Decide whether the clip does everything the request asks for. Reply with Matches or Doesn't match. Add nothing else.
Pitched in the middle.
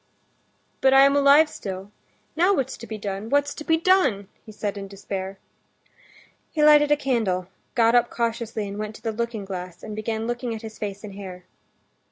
Doesn't match